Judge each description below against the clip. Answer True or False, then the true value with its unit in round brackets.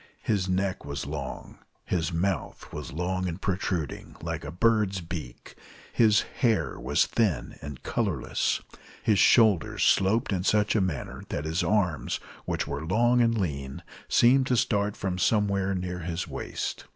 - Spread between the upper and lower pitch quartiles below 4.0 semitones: False (4.4 semitones)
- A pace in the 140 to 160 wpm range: True (150 wpm)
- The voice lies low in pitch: True (95 Hz)